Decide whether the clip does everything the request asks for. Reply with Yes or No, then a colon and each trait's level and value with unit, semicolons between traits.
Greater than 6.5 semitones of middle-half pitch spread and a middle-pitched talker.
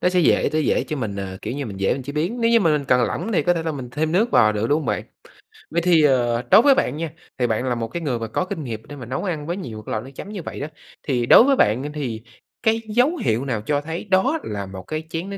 Yes: wide, 7.0 semitones; medium, 145 Hz